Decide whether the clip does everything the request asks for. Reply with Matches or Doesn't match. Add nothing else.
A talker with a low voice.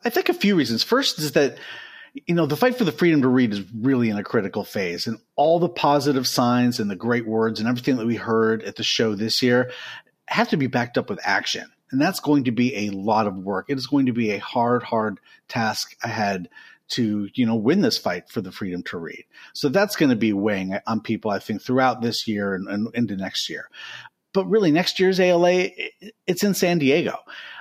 Matches